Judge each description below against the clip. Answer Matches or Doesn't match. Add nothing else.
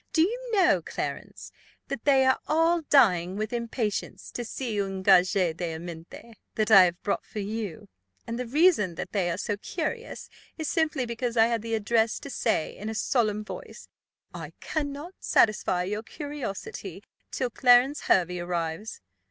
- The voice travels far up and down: Matches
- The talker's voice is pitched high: Matches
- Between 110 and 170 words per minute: Matches